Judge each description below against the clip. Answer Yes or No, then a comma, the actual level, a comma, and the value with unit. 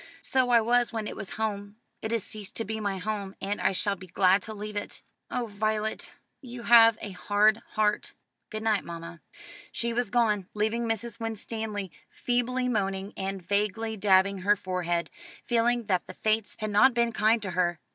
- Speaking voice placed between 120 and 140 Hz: No, high, 215 Hz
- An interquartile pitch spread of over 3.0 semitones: No, average, 2.7 semitones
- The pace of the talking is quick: No, average, 185 wpm